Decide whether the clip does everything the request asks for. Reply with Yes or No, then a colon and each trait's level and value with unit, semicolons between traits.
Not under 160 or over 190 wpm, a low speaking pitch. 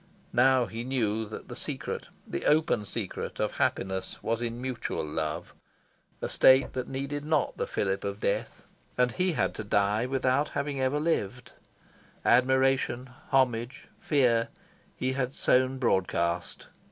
No: average, 140 wpm; low, 125 Hz